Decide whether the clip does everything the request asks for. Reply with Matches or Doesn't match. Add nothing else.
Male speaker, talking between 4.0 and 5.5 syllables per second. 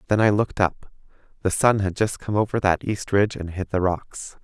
Matches